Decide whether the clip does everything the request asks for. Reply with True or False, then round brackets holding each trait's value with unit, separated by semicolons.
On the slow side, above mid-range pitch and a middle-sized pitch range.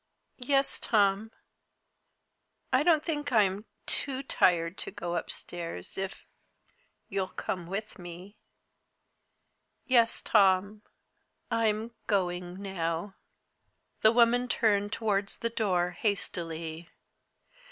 True (95 wpm; 200 Hz; 4.3 semitones)